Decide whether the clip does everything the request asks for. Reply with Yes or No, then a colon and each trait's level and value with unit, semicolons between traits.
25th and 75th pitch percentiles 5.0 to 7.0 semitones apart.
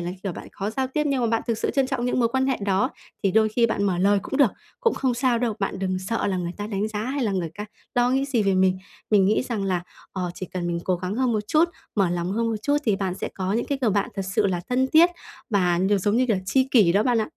No: average, 4.6 semitones